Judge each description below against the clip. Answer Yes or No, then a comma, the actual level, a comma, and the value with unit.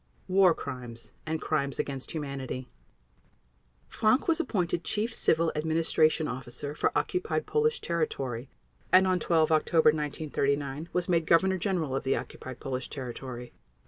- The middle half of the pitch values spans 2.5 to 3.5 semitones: No, average, 4.7 semitones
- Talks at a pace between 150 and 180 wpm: No, slow, 135 wpm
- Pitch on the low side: No, medium, 155 Hz